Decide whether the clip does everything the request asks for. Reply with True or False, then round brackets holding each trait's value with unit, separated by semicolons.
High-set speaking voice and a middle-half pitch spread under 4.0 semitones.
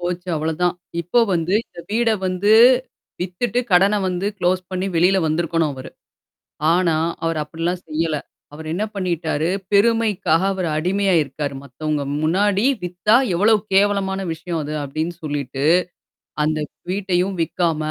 False (175 Hz; 3.3 semitones)